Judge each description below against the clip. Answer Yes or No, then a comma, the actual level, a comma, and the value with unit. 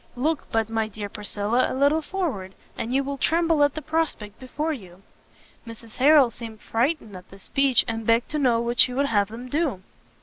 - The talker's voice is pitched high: Yes, high, 245 Hz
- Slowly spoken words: No, average, 200 wpm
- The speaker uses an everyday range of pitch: Yes, average, 4.7 semitones